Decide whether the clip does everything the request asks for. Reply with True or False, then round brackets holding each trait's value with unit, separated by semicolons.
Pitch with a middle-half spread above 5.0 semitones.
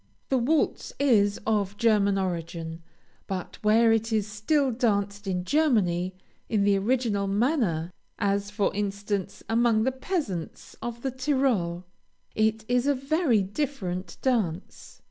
False (4.2 semitones)